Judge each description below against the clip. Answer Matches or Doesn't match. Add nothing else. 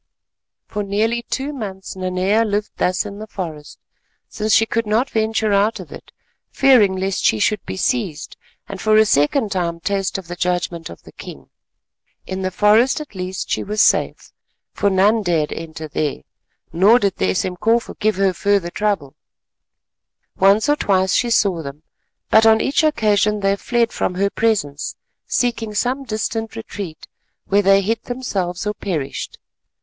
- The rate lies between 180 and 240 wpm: Doesn't match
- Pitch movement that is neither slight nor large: Matches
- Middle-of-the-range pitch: Doesn't match